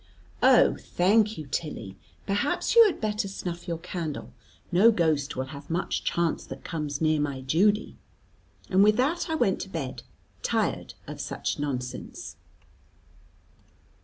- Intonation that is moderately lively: No, wide, 6.2 semitones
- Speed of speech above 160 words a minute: No, average, 140 wpm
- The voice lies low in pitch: No, medium, 170 Hz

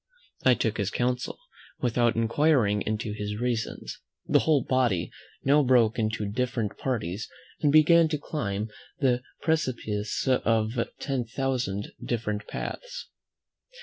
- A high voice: No, low, 120 Hz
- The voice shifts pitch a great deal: No, average, 3.8 semitones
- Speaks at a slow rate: Yes, slow, 120 wpm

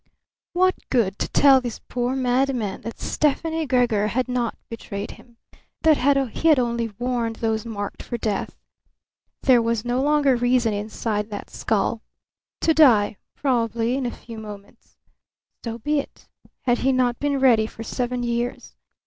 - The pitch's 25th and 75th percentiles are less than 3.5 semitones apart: Yes, average, 2.7 semitones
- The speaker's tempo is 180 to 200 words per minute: No, average, 155 wpm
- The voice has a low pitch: No, high, 240 Hz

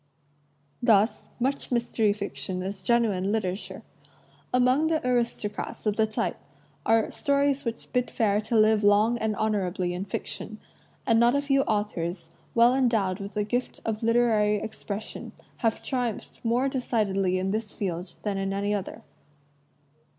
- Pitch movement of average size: Yes, average, 3.1 semitones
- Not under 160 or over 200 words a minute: No, average, 145 wpm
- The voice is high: Yes, high, 215 Hz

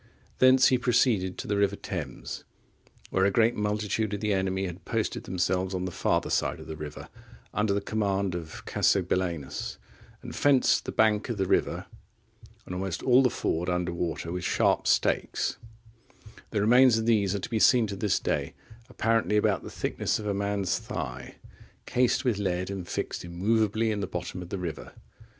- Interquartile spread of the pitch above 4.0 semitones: No, average, 3.3 semitones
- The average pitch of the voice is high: No, low, 100 Hz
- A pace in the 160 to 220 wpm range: Yes, average, 180 wpm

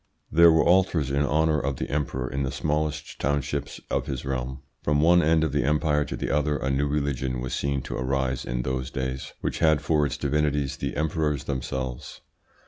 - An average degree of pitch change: No, narrow, 2.3 semitones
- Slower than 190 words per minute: No, average, 200 wpm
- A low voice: Yes, very low, 70 Hz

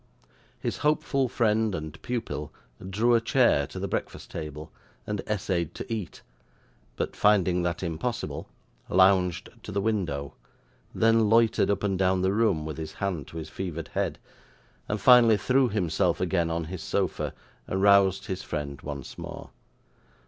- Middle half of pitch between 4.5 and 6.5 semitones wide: Yes, average, 4.8 semitones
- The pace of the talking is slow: No, average, 155 wpm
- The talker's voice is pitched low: Yes, very low, 95 Hz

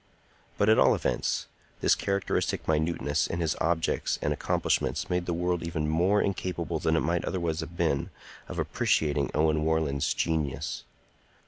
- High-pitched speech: No, very low, 80 Hz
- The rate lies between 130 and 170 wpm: Yes, average, 150 wpm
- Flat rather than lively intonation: Yes, narrow, 2.0 semitones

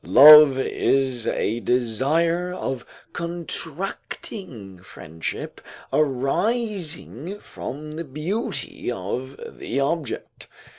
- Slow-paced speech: Yes, slow, 80 wpm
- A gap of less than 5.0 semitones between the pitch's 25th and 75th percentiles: No, wide, 5.4 semitones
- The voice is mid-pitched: Yes, medium, 145 Hz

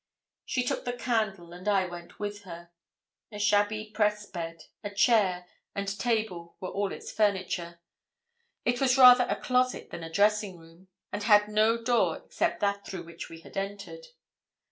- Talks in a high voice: Yes, high, 205 Hz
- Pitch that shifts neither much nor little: Yes, average, 3.5 semitones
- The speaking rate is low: No, average, 170 wpm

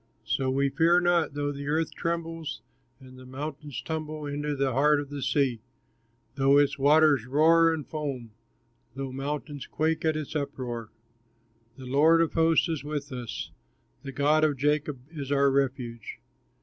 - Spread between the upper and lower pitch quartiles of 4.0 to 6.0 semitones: No, narrow, 2.4 semitones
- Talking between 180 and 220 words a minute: No, average, 155 wpm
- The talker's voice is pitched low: No, medium, 145 Hz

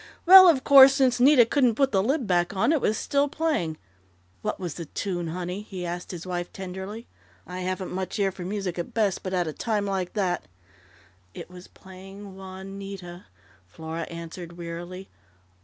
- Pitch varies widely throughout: No, average, 3.5 semitones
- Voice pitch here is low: No, high, 190 Hz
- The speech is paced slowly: No, average, 180 wpm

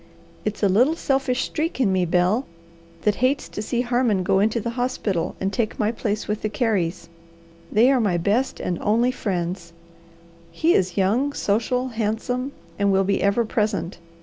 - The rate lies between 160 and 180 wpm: Yes, average, 175 wpm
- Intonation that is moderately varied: Yes, average, 4.4 semitones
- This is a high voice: Yes, high, 215 Hz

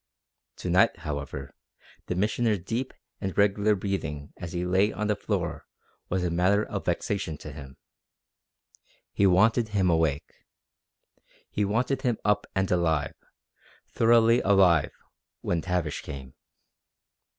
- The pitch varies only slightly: No, average, 4.4 semitones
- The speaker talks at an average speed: No, slow, 130 wpm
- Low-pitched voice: Yes, very low, 95 Hz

